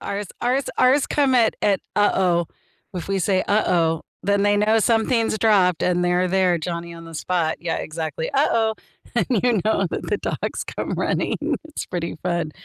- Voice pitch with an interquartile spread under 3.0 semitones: No, average, 4.4 semitones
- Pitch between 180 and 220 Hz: Yes, high, 190 Hz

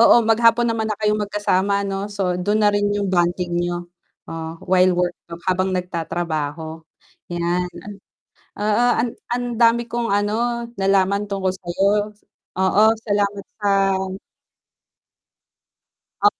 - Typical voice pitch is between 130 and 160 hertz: No, high, 195 Hz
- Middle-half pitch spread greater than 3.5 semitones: No, average, 2.8 semitones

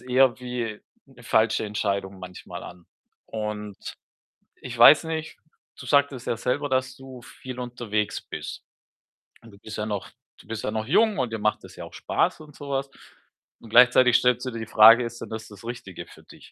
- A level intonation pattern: No, average, 3.2 semitones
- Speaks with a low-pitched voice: Yes, low, 120 Hz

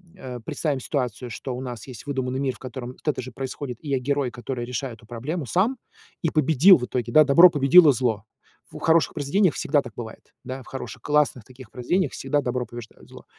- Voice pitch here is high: No, low, 130 Hz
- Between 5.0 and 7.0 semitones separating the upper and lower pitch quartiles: No, average, 3.2 semitones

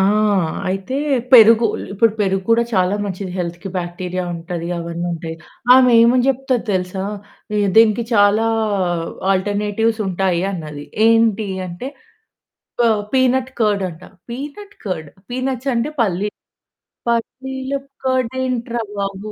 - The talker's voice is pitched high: Yes, high, 210 Hz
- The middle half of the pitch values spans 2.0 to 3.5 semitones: No, average, 4.9 semitones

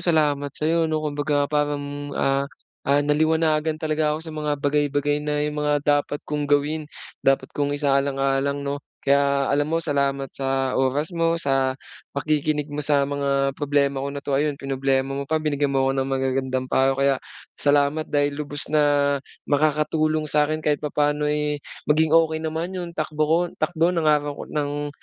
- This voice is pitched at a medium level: Yes, medium, 145 Hz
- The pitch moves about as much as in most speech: No, narrow, 1.6 semitones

